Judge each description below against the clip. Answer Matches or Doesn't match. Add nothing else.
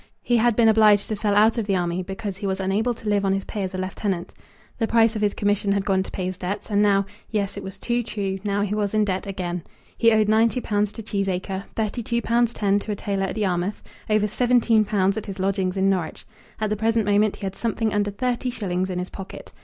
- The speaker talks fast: Matches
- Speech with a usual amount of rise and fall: Doesn't match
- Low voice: Doesn't match